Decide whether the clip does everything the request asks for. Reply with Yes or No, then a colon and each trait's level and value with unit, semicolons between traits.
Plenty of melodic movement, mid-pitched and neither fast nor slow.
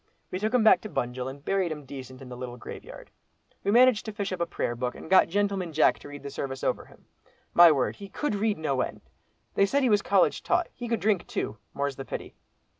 No: wide, 7.3 semitones; medium, 175 Hz; fast, 245 wpm